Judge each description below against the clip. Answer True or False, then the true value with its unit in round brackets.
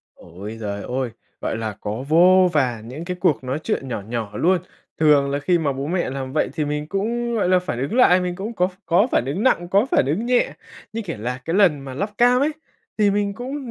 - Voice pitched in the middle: True (165 Hz)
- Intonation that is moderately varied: False (7.3 semitones)